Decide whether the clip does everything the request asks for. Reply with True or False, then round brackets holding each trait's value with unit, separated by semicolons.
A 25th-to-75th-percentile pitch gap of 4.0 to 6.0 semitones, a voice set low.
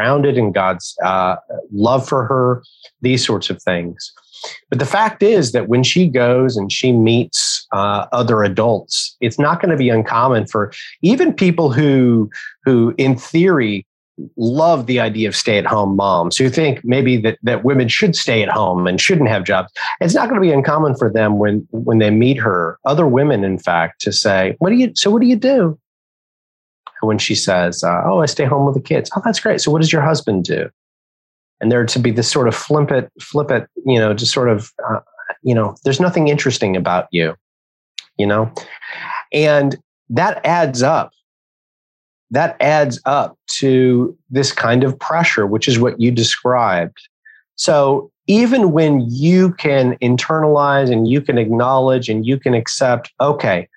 True (5.0 semitones; 125 Hz)